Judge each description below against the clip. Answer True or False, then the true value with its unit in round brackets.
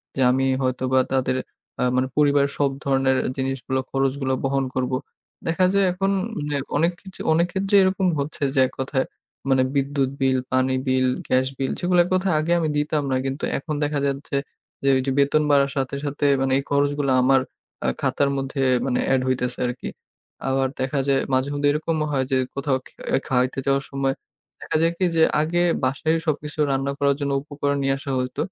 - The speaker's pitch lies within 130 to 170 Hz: True (140 Hz)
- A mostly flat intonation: True (2.0 semitones)